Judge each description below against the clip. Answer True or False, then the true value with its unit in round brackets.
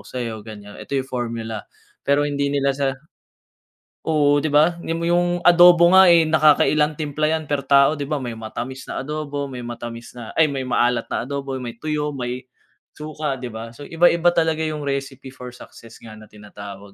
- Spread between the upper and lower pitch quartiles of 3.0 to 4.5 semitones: True (4.0 semitones)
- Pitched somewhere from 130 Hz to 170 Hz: True (140 Hz)